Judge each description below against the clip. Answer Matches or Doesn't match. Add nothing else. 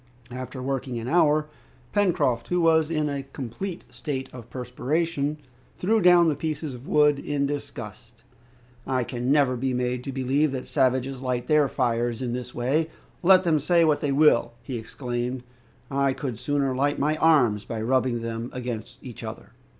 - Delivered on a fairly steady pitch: Doesn't match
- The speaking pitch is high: Doesn't match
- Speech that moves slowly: Doesn't match